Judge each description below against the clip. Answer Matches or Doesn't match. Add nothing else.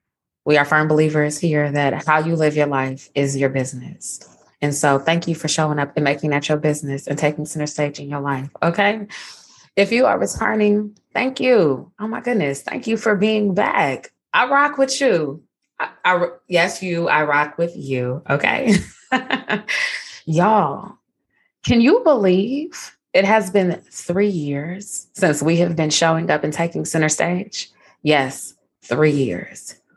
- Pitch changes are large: Matches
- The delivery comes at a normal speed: Matches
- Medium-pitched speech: Matches